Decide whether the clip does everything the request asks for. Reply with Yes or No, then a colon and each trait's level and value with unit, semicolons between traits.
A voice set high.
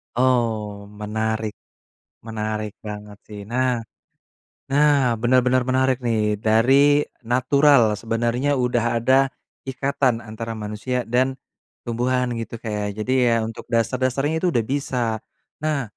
No: low, 120 Hz